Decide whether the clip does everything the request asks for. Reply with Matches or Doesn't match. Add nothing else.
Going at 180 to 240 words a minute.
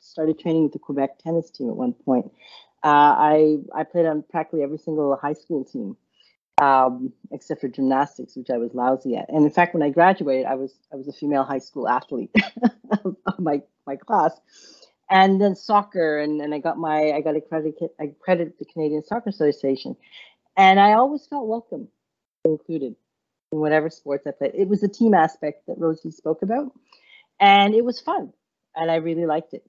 Matches